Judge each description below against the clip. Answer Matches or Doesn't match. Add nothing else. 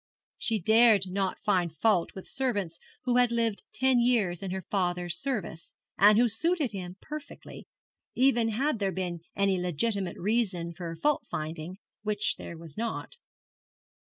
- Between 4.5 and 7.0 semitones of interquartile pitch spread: Matches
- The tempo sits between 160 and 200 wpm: Doesn't match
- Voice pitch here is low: Doesn't match